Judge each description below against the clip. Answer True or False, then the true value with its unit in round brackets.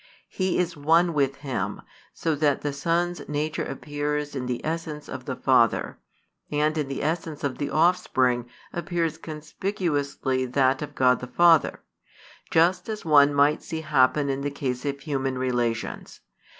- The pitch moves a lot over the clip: False (3.4 semitones)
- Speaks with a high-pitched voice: False (145 Hz)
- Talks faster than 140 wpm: True (155 wpm)